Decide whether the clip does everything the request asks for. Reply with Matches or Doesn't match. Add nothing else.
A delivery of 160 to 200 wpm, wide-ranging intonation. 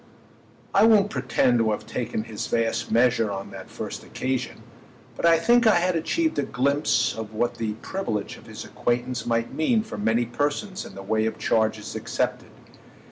Matches